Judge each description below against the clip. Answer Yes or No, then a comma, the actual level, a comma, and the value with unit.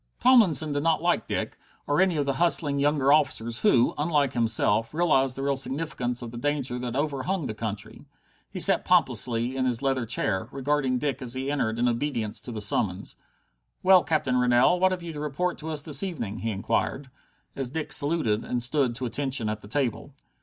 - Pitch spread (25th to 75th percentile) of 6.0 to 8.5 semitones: No, average, 3.9 semitones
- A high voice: No, low, 135 Hz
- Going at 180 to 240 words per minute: Yes, average, 195 wpm